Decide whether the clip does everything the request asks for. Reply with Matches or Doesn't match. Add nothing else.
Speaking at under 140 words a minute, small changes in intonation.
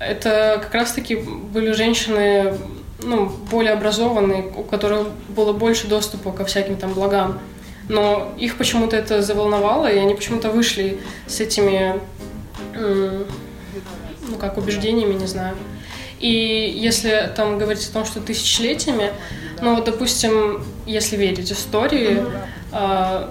Matches